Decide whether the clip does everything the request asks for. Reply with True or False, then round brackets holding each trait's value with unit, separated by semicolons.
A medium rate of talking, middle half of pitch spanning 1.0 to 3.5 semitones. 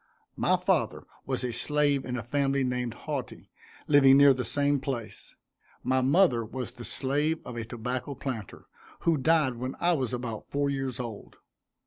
True (165 wpm; 2.5 semitones)